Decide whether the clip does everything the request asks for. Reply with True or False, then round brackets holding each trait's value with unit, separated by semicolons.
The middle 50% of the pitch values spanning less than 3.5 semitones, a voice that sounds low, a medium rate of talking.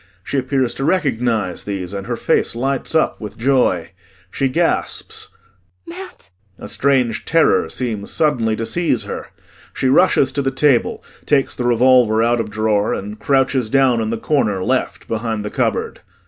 False (3.8 semitones; 120 Hz; 160 wpm)